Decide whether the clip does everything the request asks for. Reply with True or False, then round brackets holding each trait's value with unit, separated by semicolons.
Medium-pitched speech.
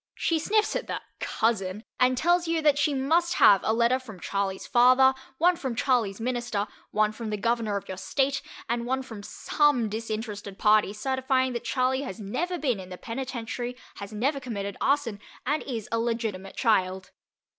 False (235 Hz)